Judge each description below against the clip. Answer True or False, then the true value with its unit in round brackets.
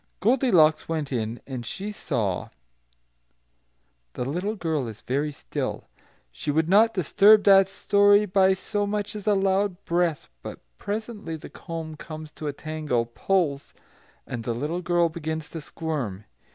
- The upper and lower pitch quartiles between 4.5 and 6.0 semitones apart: True (5.3 semitones)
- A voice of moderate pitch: True (165 Hz)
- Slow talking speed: False (150 wpm)